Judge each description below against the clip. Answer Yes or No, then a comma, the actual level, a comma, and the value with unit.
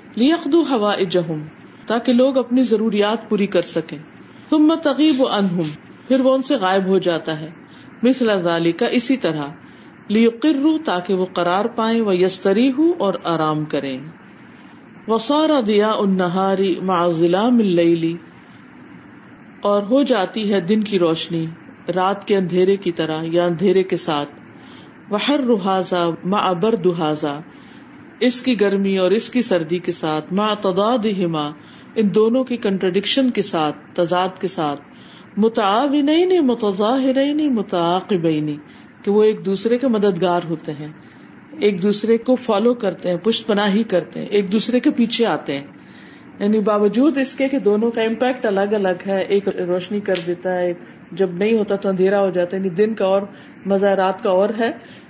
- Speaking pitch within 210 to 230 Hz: No, high, 200 Hz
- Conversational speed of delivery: Yes, average, 150 wpm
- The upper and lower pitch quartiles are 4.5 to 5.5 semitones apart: Yes, average, 5.0 semitones